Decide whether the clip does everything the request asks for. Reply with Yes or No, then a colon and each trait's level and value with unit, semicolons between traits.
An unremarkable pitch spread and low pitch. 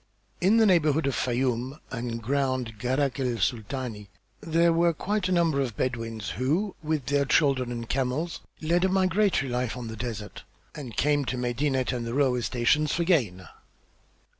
Yes: average, 4.7 semitones; low, 130 Hz